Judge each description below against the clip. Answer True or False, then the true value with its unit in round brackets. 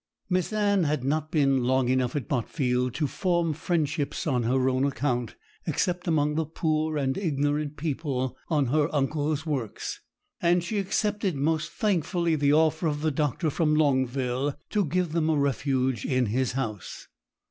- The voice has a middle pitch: True (150 Hz)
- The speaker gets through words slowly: False (160 wpm)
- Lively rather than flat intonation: False (3.6 semitones)